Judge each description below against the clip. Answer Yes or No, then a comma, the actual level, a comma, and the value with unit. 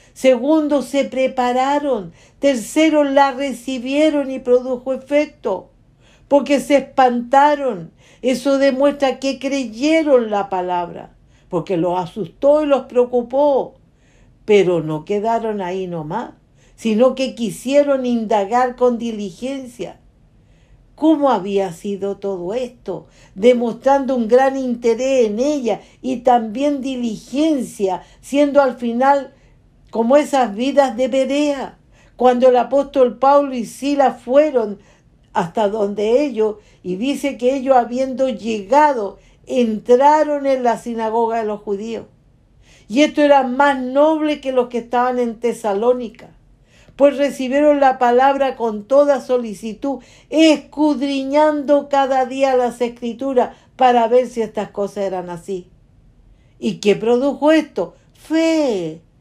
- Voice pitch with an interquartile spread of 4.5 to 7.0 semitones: No, average, 4.1 semitones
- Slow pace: Yes, slow, 115 wpm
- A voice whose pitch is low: No, very high, 250 Hz